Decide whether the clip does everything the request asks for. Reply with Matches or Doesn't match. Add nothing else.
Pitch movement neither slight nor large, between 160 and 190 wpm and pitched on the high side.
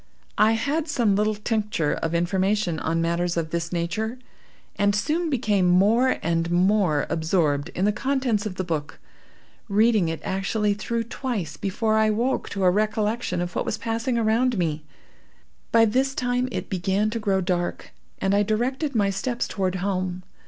Matches